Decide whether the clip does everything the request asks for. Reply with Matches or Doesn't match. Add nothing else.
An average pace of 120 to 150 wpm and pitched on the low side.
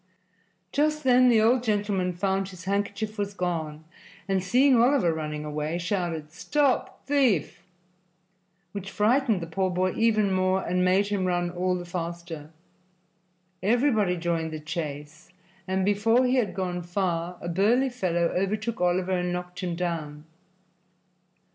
Doesn't match